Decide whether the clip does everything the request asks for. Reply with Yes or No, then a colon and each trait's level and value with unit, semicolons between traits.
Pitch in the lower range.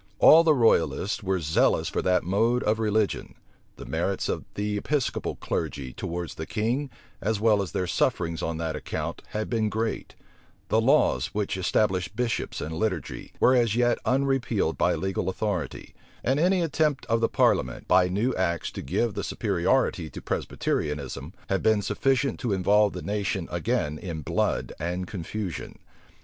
Yes: low, 105 Hz